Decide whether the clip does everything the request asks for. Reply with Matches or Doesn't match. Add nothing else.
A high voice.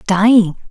Matches